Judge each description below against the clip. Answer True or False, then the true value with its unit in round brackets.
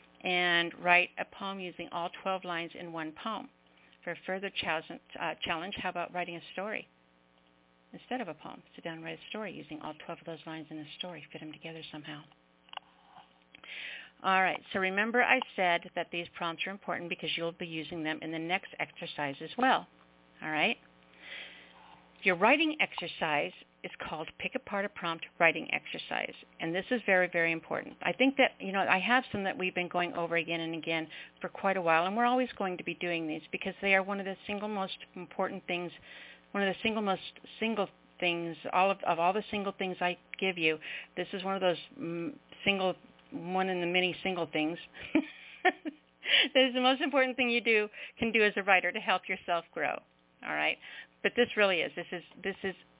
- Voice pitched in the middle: True (180 Hz)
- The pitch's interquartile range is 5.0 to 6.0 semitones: False (3.3 semitones)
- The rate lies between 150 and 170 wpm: False (205 wpm)